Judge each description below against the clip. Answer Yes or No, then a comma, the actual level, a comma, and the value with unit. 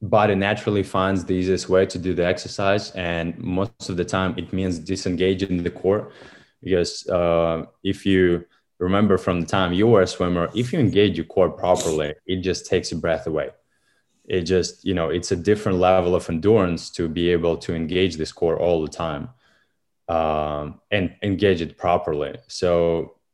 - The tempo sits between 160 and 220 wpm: Yes, average, 180 wpm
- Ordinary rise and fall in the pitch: No, narrow, 2.2 semitones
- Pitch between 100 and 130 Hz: No, very low, 90 Hz